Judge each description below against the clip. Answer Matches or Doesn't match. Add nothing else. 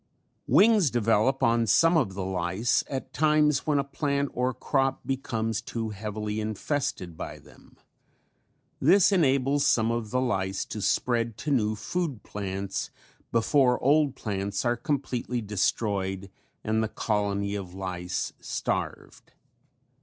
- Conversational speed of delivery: Doesn't match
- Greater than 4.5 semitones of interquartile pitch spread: Matches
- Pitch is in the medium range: Doesn't match